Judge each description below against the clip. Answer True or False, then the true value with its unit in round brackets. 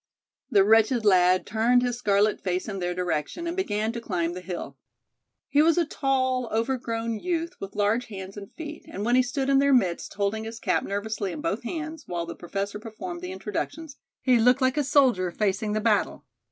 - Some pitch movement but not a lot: True (4.9 semitones)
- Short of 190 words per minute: False (200 wpm)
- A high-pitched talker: True (220 Hz)